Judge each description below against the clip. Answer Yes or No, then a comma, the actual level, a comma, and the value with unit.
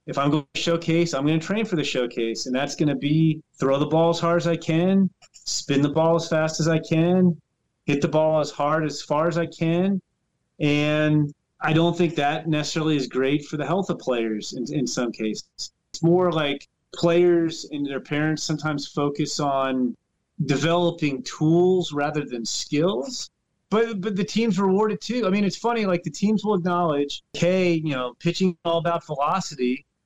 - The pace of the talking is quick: No, average, 195 wpm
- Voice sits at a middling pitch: Yes, medium, 160 Hz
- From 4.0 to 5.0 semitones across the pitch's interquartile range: No, average, 3.2 semitones